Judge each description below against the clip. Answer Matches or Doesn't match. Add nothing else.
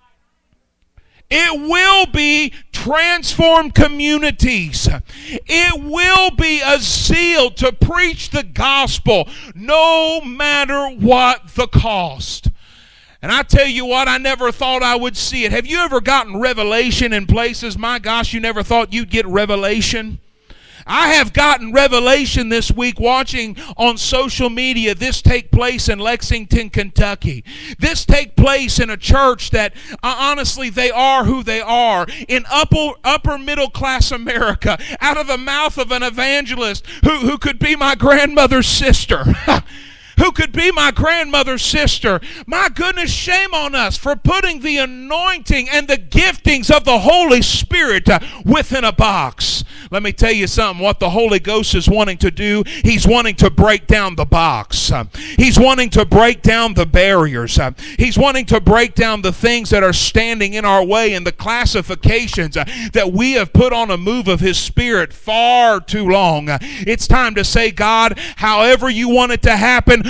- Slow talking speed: Doesn't match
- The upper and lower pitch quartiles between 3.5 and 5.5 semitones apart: Matches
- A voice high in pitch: Matches